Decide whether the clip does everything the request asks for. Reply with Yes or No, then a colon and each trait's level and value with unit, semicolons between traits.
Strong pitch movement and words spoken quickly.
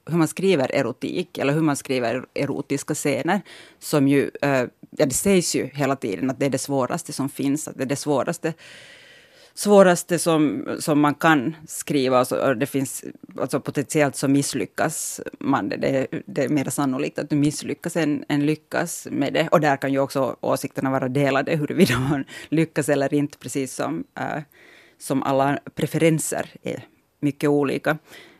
No: narrow, 2.4 semitones; fast, 170 wpm